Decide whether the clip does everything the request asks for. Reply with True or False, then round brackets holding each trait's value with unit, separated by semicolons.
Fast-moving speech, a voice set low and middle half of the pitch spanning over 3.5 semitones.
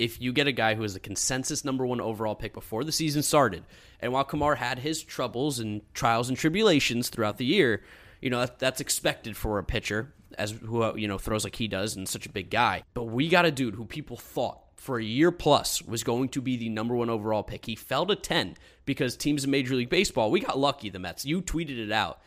True (240 wpm; 120 Hz; 4.1 semitones)